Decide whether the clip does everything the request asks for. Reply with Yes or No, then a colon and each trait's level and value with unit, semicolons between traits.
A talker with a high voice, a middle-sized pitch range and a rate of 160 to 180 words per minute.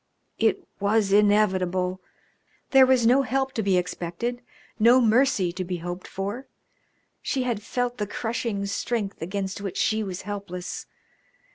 No: high, 205 Hz; average, 4.2 semitones; average, 140 wpm